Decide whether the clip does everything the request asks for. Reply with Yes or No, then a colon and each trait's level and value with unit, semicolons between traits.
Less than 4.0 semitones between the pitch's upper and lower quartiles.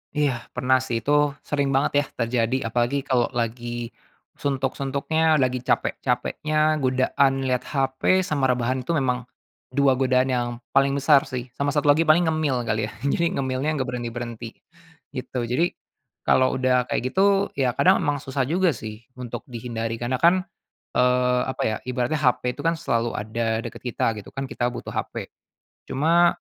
Yes: average, 3.0 semitones